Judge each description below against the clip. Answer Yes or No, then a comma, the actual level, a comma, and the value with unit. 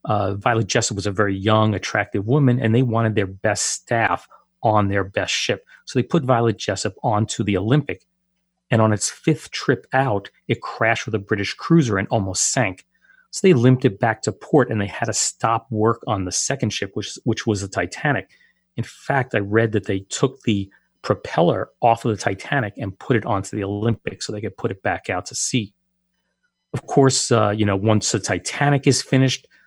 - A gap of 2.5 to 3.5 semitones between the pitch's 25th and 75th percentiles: No, average, 4.3 semitones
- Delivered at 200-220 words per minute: Yes, fast, 205 wpm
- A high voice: No, low, 115 Hz